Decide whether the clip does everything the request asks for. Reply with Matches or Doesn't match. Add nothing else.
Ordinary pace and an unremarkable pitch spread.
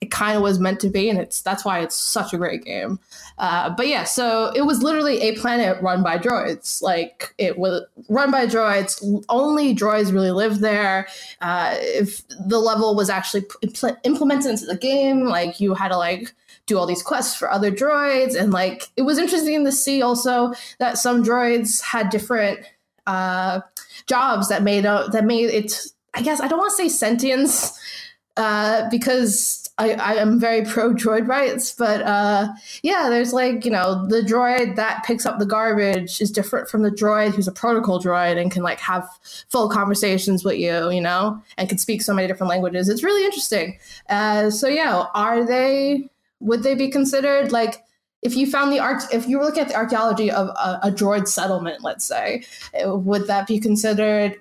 Matches